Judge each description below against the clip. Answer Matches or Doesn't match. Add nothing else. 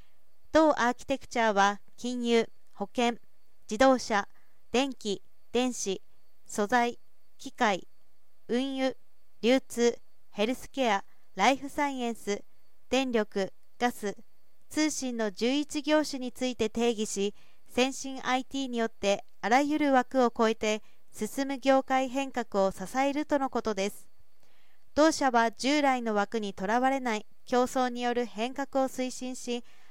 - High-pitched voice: Matches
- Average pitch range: Matches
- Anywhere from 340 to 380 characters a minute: Doesn't match